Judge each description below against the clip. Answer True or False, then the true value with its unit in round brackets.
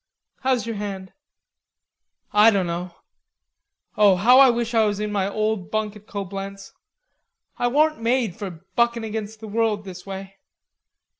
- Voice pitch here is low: False (210 Hz)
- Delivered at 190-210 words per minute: False (145 wpm)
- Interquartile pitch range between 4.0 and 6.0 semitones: False (2.8 semitones)